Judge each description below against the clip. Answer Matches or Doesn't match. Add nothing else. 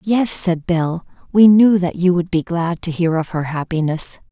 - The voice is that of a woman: Matches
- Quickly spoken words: Matches